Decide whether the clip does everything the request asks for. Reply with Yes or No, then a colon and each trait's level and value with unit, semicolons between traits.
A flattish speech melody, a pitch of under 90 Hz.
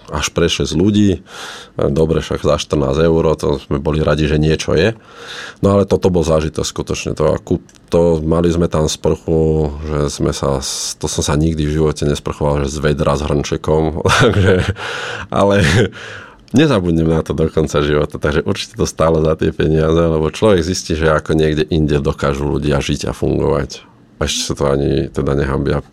Yes: narrow, 2.1 semitones; very low, 80 Hz